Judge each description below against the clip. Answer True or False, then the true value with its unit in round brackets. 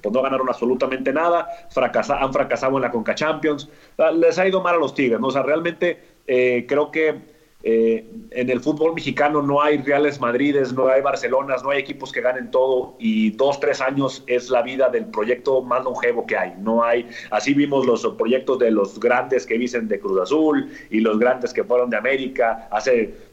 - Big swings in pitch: False (3.8 semitones)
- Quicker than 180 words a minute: True (205 wpm)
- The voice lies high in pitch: False (135 Hz)